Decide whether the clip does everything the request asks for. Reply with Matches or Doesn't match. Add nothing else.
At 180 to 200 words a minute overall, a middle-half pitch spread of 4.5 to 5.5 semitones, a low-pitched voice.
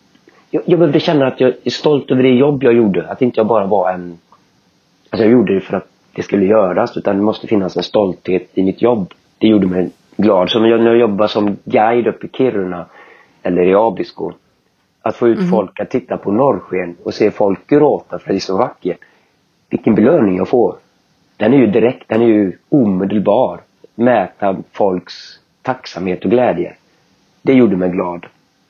Matches